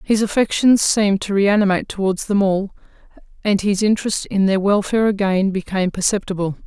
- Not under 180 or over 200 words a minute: No, average, 155 wpm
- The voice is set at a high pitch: Yes, high, 200 Hz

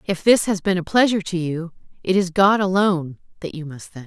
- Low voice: No, medium, 180 Hz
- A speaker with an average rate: No, fast, 235 wpm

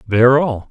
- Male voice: Yes, male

